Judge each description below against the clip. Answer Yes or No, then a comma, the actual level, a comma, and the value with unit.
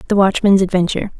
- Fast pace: No, average, 150 wpm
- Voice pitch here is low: No, high, 190 Hz